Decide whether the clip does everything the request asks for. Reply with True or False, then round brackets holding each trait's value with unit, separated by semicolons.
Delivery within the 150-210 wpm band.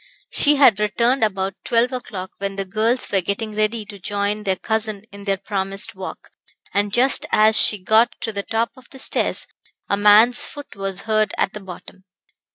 True (185 wpm)